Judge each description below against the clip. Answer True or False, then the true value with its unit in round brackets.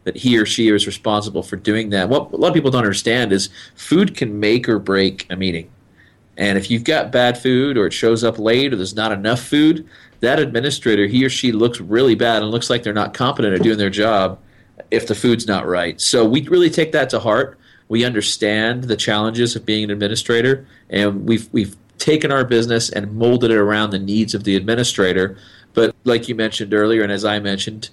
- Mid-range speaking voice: False (110 Hz)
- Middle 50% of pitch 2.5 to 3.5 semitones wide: True (2.9 semitones)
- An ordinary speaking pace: False (220 wpm)